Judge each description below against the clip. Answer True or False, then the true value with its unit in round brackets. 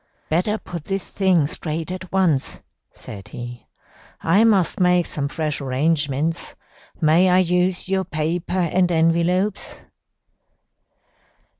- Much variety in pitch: False (3.1 semitones)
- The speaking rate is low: True (115 wpm)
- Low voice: False (170 Hz)